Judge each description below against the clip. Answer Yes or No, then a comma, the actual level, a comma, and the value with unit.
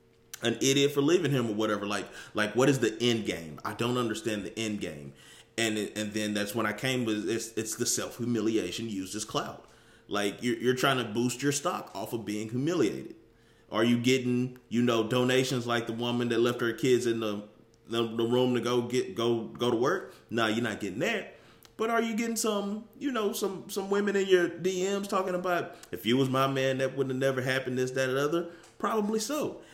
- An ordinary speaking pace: No, fast, 220 wpm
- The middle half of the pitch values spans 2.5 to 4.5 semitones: Yes, average, 3.6 semitones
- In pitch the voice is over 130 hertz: No, low, 120 Hz